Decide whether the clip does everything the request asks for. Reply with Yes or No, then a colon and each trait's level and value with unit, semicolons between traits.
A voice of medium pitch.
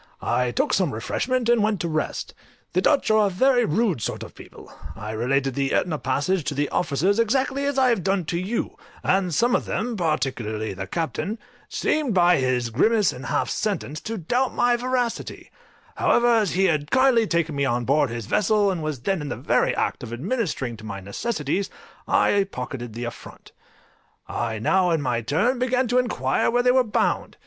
Yes: medium, 180 Hz